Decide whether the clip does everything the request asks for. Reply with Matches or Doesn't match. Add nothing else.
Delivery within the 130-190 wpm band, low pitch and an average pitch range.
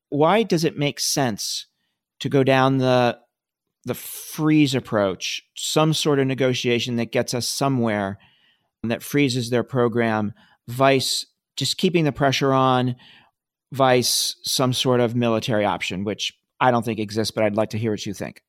Matches